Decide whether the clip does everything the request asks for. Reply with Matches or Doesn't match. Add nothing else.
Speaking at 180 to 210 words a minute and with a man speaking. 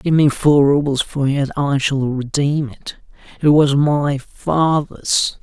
Doesn't match